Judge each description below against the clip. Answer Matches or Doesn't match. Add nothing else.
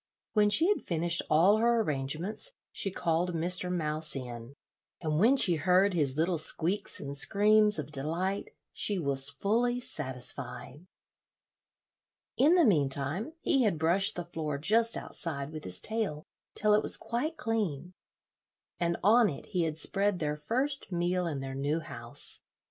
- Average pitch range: Doesn't match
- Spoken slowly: Doesn't match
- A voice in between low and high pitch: Matches